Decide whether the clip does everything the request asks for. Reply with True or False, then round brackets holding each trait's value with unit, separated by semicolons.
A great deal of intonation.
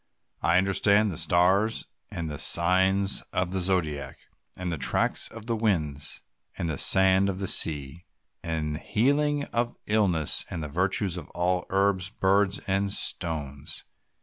False (3.4 semitones)